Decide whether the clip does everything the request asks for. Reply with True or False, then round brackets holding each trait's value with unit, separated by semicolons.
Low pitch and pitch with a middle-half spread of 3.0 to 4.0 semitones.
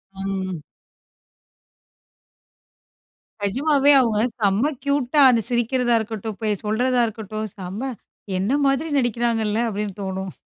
False (220 Hz; 3.7 semitones)